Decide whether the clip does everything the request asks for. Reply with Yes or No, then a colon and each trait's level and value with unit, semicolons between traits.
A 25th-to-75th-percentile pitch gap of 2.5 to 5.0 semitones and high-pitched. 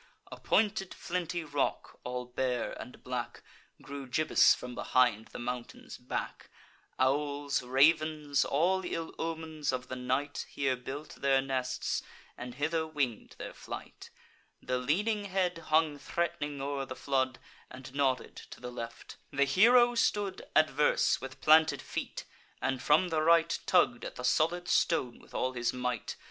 No: average, 4.1 semitones; medium, 140 Hz